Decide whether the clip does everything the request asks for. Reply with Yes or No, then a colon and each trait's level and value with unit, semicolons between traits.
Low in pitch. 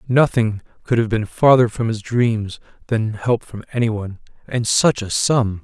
Yes: low, 115 Hz